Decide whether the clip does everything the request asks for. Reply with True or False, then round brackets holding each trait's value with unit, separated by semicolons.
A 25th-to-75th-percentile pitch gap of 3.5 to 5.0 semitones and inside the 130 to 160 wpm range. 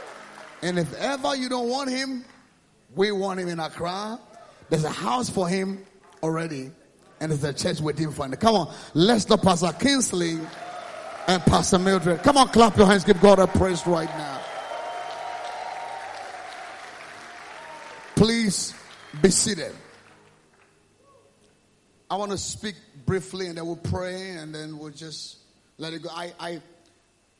True (4.6 semitones; 145 wpm)